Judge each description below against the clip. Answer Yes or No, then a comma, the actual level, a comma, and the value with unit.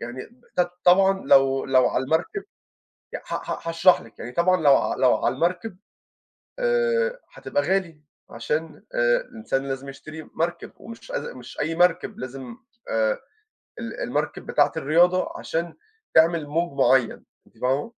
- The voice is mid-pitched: Yes, medium, 165 Hz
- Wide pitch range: Yes, wide, 6.2 semitones